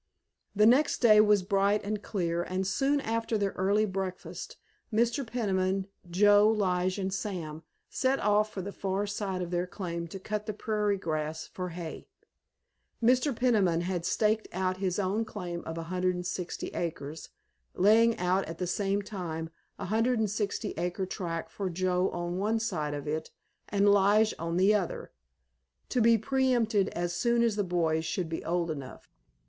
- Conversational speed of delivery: Yes, average, 165 wpm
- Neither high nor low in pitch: No, high, 195 Hz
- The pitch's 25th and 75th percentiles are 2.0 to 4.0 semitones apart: Yes, average, 3.3 semitones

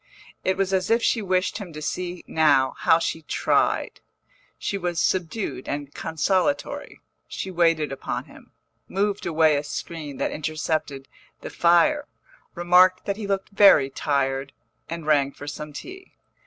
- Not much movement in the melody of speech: No, average, 4.2 semitones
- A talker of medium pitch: Yes, medium, 170 Hz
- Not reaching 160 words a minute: Yes, average, 150 wpm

